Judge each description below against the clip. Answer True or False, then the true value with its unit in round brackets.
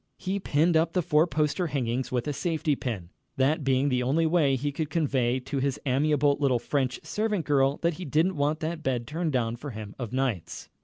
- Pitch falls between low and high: True (145 Hz)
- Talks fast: True (210 wpm)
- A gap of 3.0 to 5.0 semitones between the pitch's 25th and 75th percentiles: True (3.6 semitones)